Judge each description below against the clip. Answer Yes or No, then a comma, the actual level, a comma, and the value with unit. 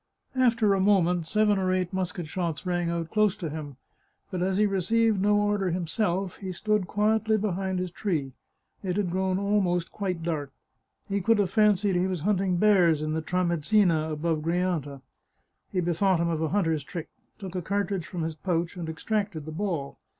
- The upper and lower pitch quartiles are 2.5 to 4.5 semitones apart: Yes, average, 3.3 semitones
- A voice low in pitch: No, medium, 185 Hz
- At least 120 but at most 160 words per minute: No, average, 195 wpm